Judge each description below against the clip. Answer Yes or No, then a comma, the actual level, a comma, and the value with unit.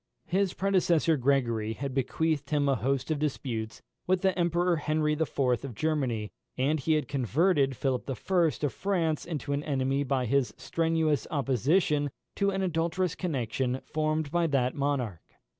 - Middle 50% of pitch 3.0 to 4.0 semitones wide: Yes, average, 3.7 semitones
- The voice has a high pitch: No, medium, 145 Hz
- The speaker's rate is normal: Yes, average, 155 wpm